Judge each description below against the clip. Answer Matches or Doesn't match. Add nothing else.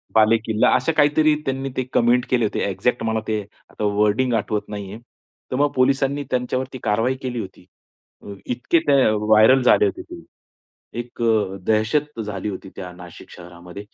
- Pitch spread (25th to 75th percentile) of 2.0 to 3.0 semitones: Doesn't match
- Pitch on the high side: Doesn't match